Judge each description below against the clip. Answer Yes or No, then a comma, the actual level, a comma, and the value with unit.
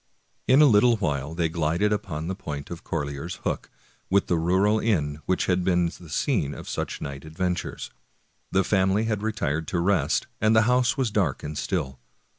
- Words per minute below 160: No, average, 185 wpm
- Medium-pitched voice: No, very low, 90 Hz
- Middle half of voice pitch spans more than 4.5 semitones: Yes, average, 5.2 semitones